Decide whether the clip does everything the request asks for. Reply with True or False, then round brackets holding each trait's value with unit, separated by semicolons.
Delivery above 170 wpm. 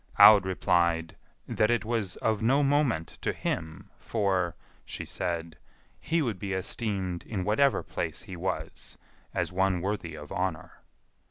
False (145 wpm)